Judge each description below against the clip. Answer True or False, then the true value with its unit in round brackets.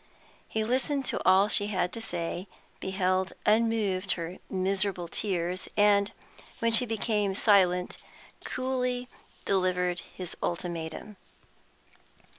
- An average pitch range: True (3.3 semitones)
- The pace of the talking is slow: True (105 wpm)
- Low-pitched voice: False (195 Hz)